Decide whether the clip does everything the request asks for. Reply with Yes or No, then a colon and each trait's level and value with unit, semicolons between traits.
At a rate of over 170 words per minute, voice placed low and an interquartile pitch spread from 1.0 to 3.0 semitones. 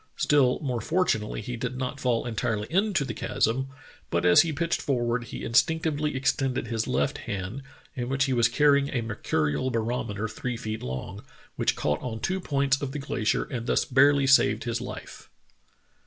No: average, 180 wpm; low, 125 Hz; average, 3.6 semitones